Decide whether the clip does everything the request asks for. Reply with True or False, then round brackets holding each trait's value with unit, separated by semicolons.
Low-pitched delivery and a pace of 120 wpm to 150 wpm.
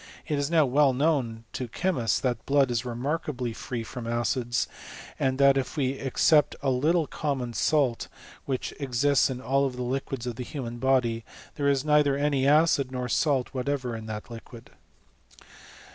False (130 Hz; 175 wpm)